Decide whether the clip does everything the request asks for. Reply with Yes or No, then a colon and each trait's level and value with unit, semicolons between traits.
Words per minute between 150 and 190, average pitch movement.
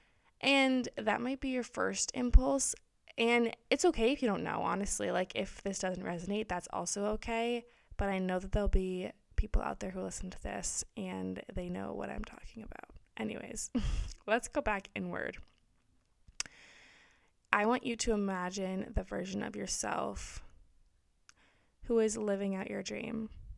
Yes: average, 160 wpm; average, 4.2 semitones